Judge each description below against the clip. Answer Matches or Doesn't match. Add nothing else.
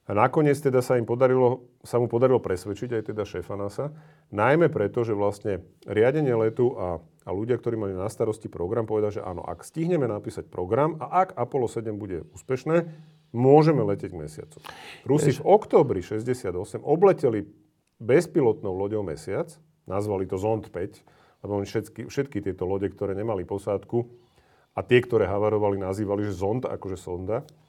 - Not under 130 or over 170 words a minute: Matches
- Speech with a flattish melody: Doesn't match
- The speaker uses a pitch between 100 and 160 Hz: Matches